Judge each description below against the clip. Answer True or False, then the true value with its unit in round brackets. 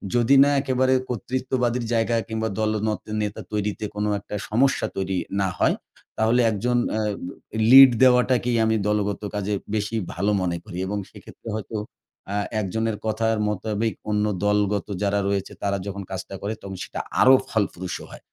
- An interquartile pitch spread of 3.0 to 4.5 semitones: False (2.6 semitones)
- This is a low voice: True (110 Hz)